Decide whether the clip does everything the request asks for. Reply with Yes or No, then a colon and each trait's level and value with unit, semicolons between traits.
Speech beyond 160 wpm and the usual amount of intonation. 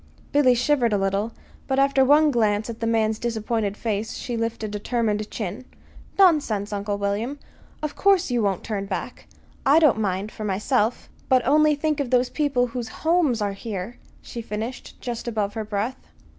Yes: average, 175 wpm; average, 4.1 semitones